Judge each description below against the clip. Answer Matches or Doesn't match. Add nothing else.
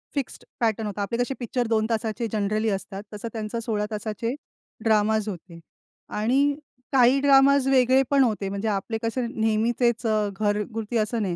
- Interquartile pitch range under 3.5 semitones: Matches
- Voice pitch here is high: Matches